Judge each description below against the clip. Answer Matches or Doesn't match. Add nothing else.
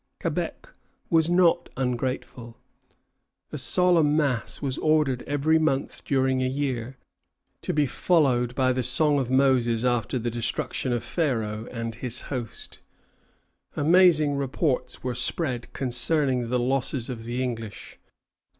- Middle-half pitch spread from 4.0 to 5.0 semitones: Doesn't match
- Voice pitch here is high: Doesn't match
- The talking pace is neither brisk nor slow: Doesn't match